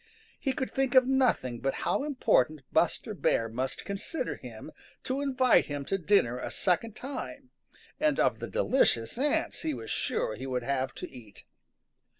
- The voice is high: Yes, high, 195 Hz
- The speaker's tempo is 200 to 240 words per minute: No, average, 165 wpm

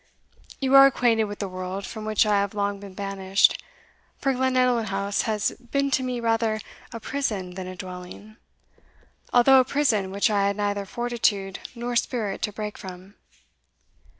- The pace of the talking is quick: No, average, 165 wpm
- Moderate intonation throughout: Yes, average, 3.5 semitones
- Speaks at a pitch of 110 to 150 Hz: No, high, 210 Hz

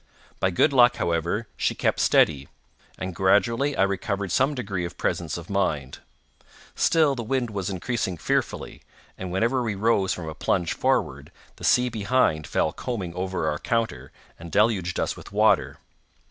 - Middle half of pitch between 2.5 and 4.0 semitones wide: No, average, 5.1 semitones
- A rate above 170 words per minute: No, average, 160 wpm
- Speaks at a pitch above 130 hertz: No, low, 100 Hz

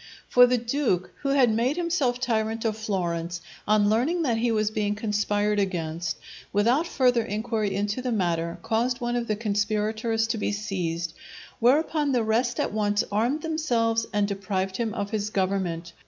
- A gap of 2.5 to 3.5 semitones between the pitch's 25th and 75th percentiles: Yes, average, 3.2 semitones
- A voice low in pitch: No, high, 220 Hz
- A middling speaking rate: Yes, average, 170 wpm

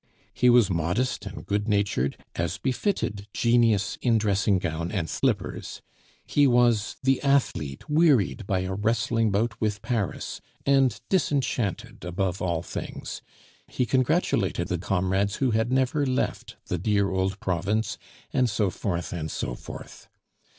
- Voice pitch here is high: No, low, 105 Hz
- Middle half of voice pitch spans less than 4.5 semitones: No, average, 4.8 semitones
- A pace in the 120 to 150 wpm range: Yes, average, 140 wpm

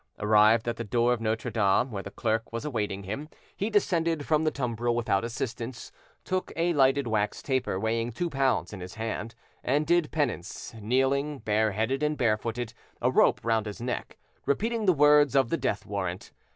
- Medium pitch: No, low, 120 Hz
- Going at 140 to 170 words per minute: No, average, 180 wpm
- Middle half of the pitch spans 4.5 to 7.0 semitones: Yes, average, 4.8 semitones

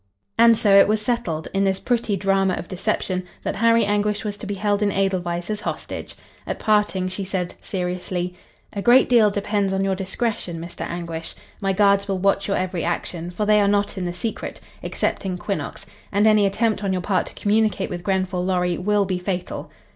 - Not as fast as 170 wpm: No, average, 200 wpm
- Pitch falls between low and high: No, high, 195 Hz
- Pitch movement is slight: Yes, narrow, 2.3 semitones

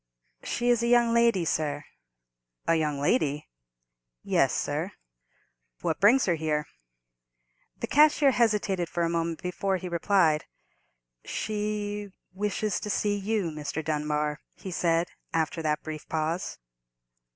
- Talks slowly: Yes, slow, 125 wpm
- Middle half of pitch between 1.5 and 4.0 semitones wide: No, average, 5.0 semitones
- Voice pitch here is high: No, medium, 175 Hz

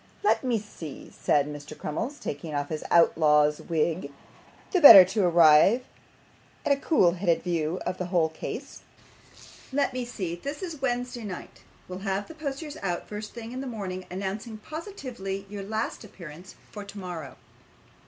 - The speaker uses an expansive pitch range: Yes, wide, 6.3 semitones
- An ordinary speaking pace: Yes, average, 160 wpm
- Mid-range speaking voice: No, high, 195 Hz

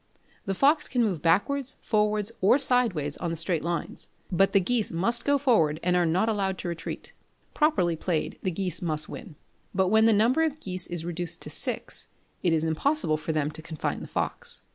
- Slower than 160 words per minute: No, average, 200 wpm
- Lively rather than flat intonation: Yes, wide, 5.8 semitones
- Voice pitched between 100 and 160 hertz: No, medium, 185 Hz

